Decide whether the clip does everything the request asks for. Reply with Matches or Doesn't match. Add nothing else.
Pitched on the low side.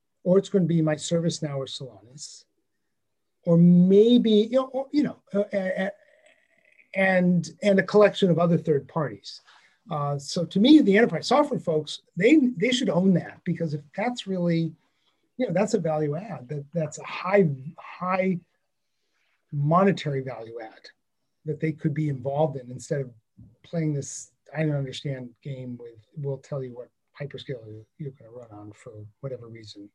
Doesn't match